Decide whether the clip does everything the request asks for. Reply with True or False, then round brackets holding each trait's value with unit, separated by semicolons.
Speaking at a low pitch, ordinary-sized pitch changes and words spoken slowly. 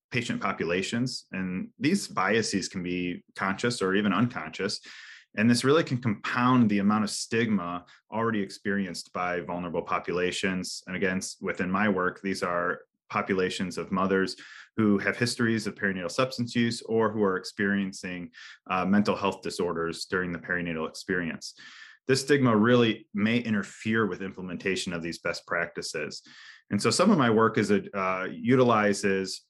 False (100 Hz; 3.6 semitones; 155 wpm)